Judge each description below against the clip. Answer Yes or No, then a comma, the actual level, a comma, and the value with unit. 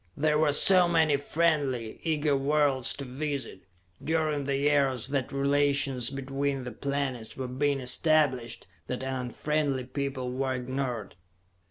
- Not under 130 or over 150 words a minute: Yes, slow, 135 wpm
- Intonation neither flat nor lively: No, narrow, 2.2 semitones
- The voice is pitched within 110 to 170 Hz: Yes, medium, 140 Hz